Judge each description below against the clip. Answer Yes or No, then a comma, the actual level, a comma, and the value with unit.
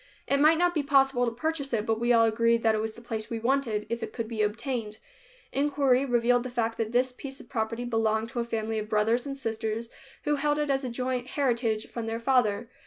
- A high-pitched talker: Yes, high, 235 Hz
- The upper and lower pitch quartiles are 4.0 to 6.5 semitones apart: No, average, 3.1 semitones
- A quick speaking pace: Yes, fast, 235 wpm